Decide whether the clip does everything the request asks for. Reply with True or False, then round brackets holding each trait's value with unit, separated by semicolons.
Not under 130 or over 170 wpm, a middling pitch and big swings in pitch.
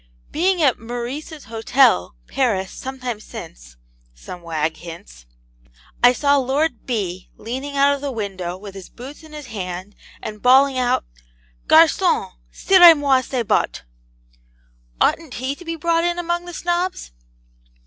False (145 wpm; 255 Hz; 7.1 semitones)